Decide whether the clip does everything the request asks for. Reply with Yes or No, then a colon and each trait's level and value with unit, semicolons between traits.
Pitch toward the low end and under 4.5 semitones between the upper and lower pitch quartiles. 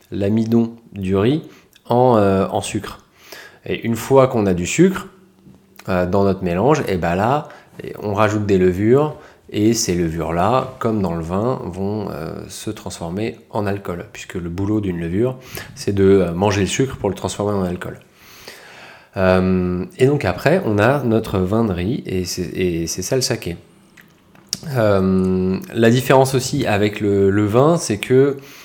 No: low, 105 Hz; average, 5.0 semitones